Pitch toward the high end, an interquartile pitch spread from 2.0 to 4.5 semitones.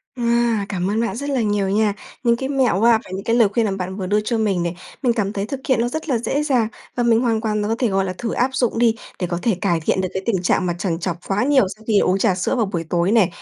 Yes: high, 215 Hz; average, 3.7 semitones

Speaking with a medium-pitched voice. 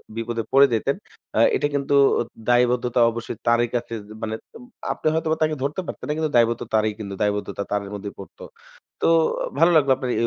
No: low, 120 Hz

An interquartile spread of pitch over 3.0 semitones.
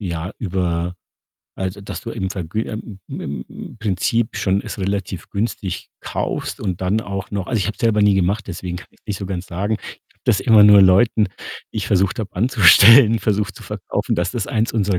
No: narrow, 2.6 semitones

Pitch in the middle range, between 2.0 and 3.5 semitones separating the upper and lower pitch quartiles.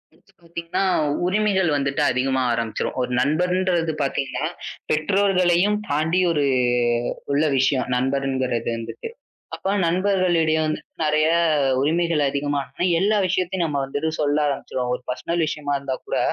No: medium, 155 Hz; average, 4.7 semitones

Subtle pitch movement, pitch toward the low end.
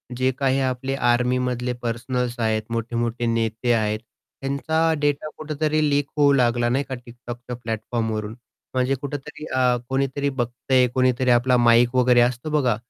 Yes: narrow, 2.3 semitones; low, 125 Hz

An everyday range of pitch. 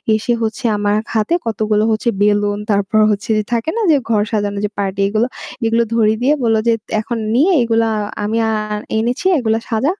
No: narrow, 1.8 semitones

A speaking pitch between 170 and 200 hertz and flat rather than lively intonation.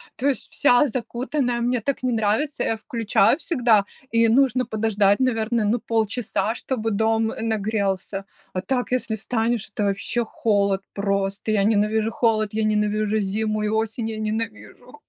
No: high, 220 Hz; narrow, 2.3 semitones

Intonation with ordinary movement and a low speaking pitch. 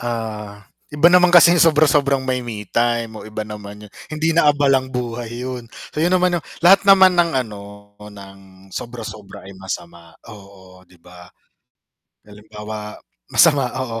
No: wide, 5.7 semitones; low, 115 Hz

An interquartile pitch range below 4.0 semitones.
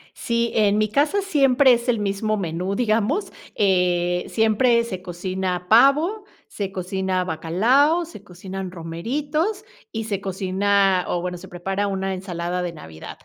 No: average, 4.6 semitones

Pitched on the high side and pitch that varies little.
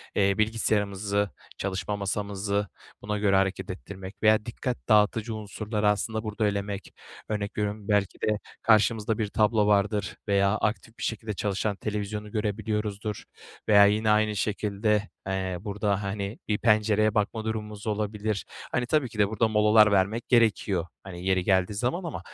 No: low, 105 Hz; narrow, 1.3 semitones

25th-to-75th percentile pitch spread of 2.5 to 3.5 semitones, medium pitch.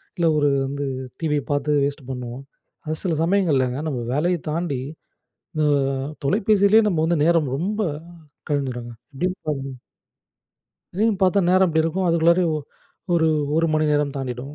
No: average, 4.4 semitones; medium, 155 Hz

